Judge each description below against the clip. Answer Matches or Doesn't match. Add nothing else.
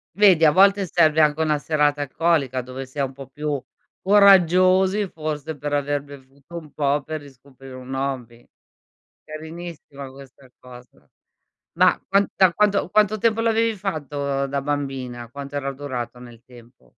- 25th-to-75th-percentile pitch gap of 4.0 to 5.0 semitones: Matches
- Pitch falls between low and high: Matches